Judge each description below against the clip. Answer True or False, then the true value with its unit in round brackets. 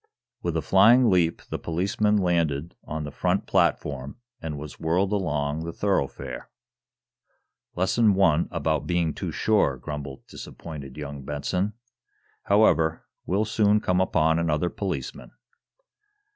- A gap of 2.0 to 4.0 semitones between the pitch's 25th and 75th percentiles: False (4.5 semitones)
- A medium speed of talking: False (130 wpm)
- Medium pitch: False (85 Hz)